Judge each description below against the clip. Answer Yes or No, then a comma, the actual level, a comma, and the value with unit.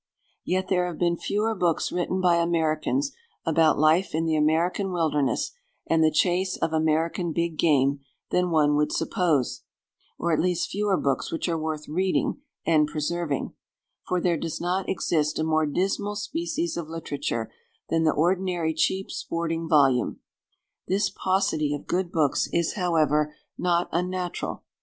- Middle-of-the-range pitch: Yes, medium, 165 Hz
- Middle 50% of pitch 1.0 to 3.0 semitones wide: Yes, average, 2.7 semitones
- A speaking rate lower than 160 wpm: Yes, average, 150 wpm